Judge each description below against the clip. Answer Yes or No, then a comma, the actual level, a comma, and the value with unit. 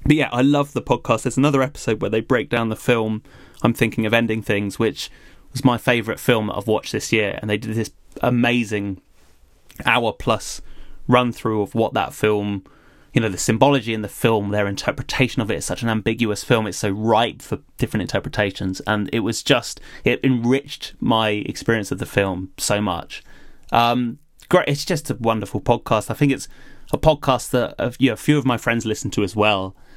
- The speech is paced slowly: No, average, 195 wpm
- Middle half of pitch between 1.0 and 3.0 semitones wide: No, average, 3.4 semitones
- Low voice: Yes, low, 115 Hz